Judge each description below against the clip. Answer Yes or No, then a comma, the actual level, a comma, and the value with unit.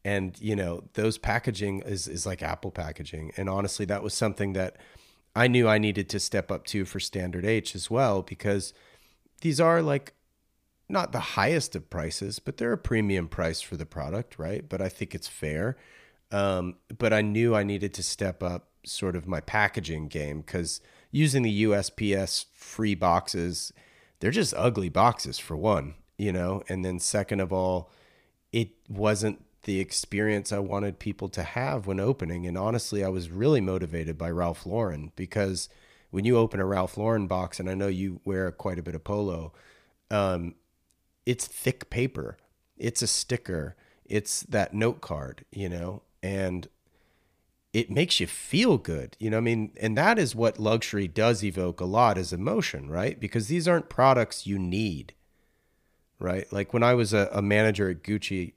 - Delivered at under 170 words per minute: No, average, 180 wpm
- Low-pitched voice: Yes, low, 100 Hz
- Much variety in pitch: No, average, 3.3 semitones